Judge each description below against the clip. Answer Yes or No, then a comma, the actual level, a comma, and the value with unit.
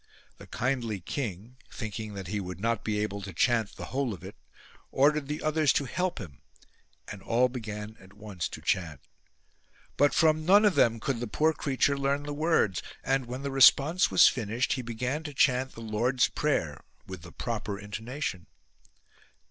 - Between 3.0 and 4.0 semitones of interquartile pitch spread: No, average, 5.1 semitones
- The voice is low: Yes, low, 120 Hz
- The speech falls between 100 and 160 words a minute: No, average, 180 wpm